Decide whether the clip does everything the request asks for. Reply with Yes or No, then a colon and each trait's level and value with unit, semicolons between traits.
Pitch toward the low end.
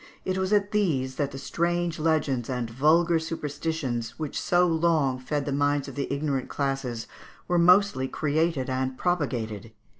No: medium, 145 Hz